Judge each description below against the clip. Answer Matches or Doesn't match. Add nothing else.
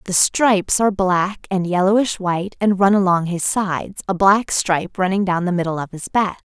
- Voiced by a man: Doesn't match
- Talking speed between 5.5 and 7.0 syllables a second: Doesn't match